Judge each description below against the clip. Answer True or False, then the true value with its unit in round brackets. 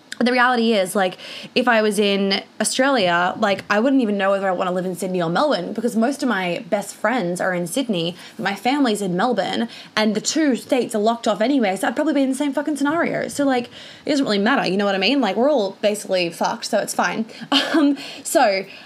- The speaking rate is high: True (240 wpm)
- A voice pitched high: True (225 Hz)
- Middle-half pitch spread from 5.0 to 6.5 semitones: True (5.6 semitones)